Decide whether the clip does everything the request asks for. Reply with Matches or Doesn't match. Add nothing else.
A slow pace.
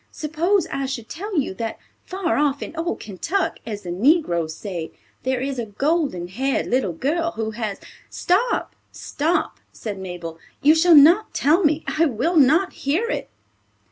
Doesn't match